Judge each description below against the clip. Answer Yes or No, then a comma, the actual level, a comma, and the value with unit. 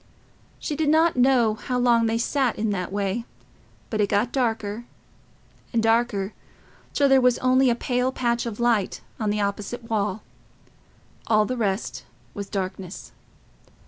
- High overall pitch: Yes, high, 230 Hz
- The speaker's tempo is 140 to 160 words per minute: Yes, average, 150 wpm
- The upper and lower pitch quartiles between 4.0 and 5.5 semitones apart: No, average, 3.2 semitones